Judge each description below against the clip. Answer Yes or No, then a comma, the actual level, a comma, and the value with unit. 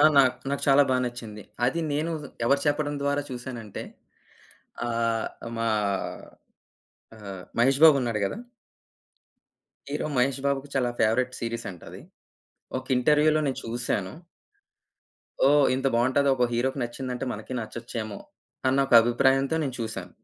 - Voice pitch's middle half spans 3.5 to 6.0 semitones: No, average, 3.0 semitones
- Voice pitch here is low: Yes, low, 130 Hz